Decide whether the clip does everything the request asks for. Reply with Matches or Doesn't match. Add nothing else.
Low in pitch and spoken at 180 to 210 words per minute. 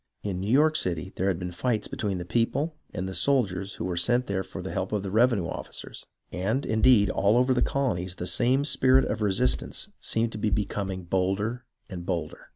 Matches